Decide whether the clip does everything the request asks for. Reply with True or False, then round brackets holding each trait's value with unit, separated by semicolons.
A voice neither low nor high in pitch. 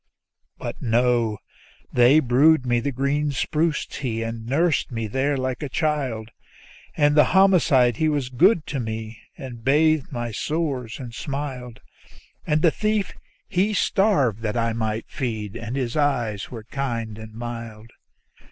False (125 Hz)